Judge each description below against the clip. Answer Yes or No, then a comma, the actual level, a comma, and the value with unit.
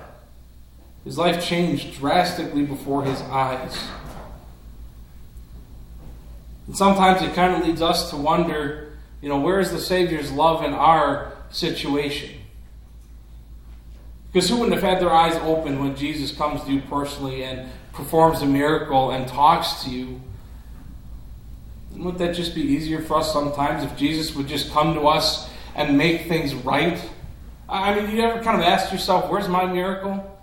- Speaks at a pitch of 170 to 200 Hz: No, medium, 150 Hz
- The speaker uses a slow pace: No, average, 155 wpm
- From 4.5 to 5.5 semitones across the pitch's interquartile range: Yes, average, 4.8 semitones